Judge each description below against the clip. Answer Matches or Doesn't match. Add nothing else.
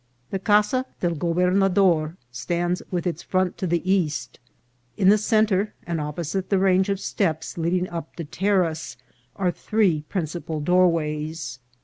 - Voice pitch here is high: Doesn't match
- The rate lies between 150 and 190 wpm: Doesn't match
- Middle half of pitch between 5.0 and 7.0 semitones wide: Doesn't match